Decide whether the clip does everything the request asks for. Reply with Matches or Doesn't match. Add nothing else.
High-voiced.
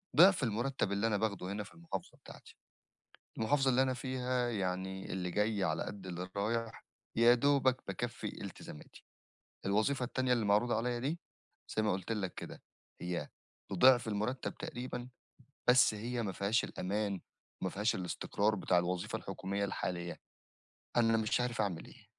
Doesn't match